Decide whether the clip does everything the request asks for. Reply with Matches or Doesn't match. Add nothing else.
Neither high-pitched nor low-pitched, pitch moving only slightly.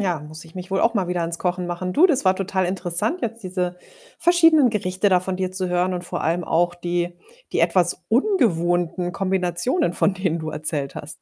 Matches